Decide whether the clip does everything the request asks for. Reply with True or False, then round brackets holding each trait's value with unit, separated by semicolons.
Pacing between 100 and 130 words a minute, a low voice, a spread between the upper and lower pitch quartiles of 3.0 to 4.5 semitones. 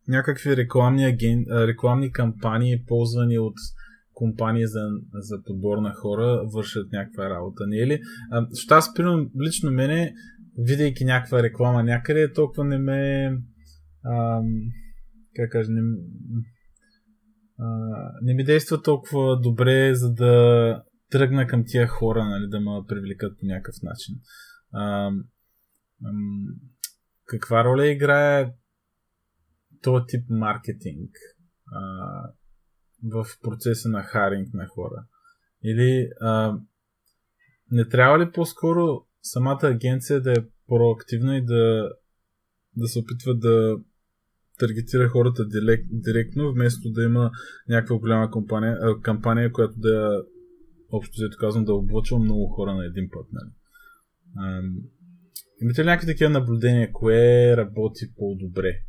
True (120 wpm; 115 Hz; 3.4 semitones)